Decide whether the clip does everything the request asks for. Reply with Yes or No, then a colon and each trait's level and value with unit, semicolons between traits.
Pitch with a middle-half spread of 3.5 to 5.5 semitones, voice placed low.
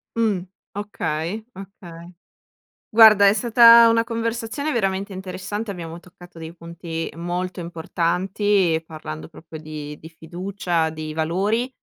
No: average, 4.2 semitones; medium, 180 Hz